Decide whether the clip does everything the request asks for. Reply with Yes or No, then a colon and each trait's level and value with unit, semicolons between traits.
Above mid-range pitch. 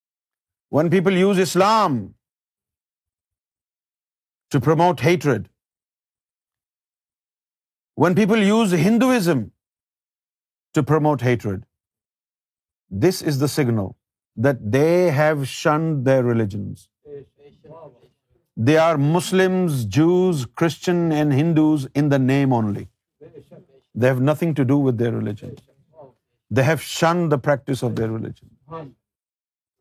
No: medium, 140 Hz